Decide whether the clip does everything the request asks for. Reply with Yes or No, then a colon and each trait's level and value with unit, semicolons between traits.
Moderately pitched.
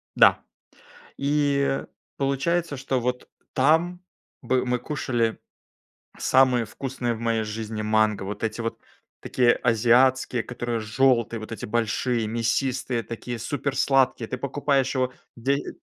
No: low, 125 Hz